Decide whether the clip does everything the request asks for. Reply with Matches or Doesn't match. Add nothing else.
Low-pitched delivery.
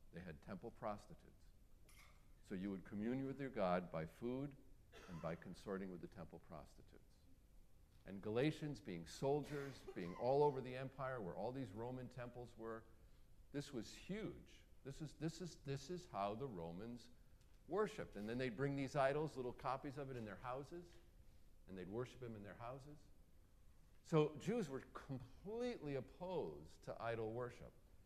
Matches